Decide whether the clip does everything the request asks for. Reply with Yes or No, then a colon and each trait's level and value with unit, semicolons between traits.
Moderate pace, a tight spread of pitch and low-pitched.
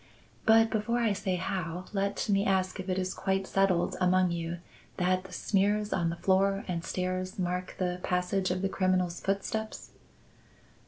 No: average, 165 wpm; narrow, 1.5 semitones; medium, 185 Hz